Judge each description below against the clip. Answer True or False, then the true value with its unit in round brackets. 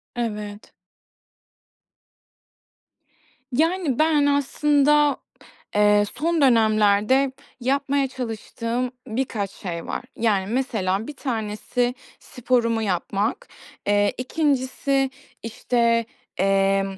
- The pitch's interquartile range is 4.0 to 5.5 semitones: True (4.8 semitones)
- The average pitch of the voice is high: True (240 Hz)